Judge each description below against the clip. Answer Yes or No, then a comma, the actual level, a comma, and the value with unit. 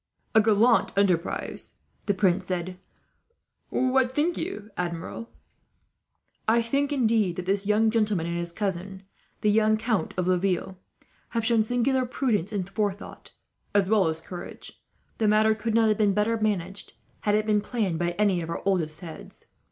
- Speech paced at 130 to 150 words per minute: No, average, 160 wpm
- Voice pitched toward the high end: Yes, high, 210 Hz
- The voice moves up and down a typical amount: Yes, average, 3.4 semitones